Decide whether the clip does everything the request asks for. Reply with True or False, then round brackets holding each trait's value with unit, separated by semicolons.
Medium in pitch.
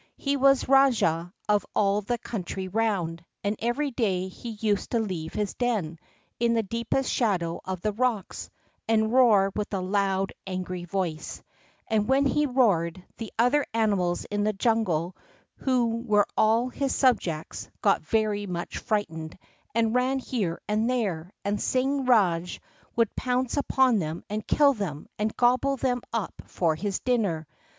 False (215 Hz)